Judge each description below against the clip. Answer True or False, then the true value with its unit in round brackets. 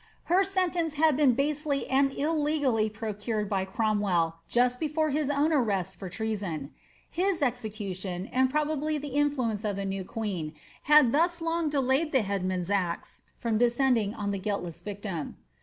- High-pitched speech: True (240 Hz)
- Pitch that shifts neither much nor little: False (6.7 semitones)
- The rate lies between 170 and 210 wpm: False (155 wpm)